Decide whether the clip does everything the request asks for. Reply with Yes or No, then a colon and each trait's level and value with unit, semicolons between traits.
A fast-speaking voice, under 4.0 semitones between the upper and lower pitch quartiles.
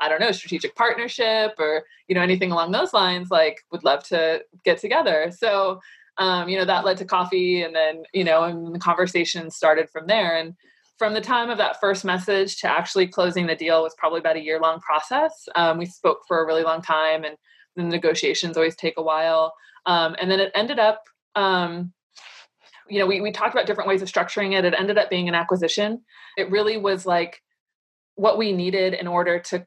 Yes: fast, 210 wpm; average, 3.6 semitones